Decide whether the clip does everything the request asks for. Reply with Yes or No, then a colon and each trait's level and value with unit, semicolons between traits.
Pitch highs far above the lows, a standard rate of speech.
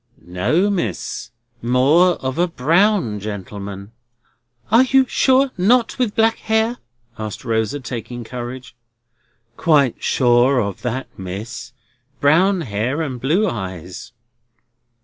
No: wide, 8.9 semitones; slow, 110 wpm